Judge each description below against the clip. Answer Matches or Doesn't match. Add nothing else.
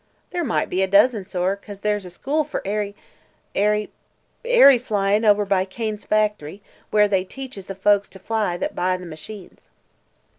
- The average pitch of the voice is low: Doesn't match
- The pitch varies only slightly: Matches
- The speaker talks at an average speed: Matches